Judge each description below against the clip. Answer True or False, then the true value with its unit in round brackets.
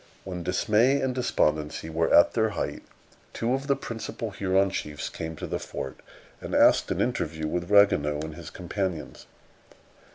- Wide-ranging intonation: True (5.8 semitones)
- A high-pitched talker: False (90 Hz)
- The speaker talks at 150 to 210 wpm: True (160 wpm)